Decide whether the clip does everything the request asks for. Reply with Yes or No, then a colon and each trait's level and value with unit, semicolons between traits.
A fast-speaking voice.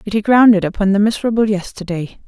Yes: fast, 210 wpm